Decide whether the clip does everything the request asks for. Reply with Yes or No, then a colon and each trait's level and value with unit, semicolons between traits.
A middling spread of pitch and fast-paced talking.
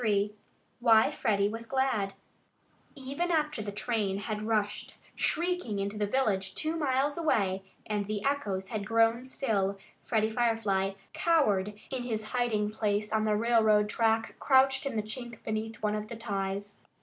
No: average, 3.2 semitones; average, 155 wpm